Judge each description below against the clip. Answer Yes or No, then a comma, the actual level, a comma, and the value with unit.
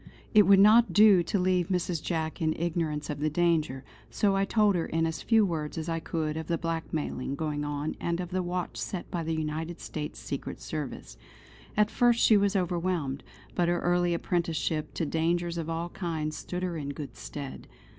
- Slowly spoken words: No, average, 195 wpm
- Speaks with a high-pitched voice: No, medium, 170 Hz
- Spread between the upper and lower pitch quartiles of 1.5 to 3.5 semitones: Yes, average, 2.7 semitones